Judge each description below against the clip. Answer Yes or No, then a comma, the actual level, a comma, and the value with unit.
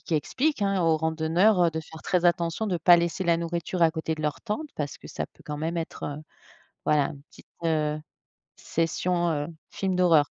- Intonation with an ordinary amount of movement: No, narrow, 2.3 semitones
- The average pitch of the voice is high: No, medium, 165 Hz